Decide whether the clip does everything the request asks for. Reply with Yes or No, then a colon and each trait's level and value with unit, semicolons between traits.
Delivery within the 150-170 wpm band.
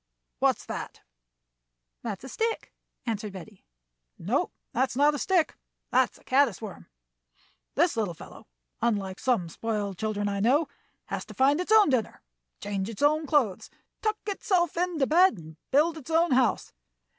Yes: average, 155 wpm